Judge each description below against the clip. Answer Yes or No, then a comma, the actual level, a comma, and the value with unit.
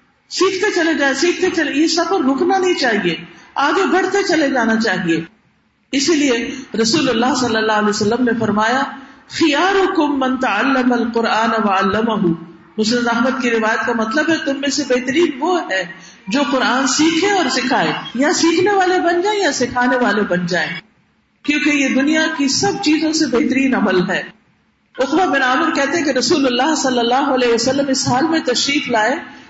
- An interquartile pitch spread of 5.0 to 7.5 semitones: Yes, wide, 5.5 semitones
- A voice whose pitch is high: Yes, very high, 265 Hz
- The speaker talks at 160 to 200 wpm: Yes, average, 170 wpm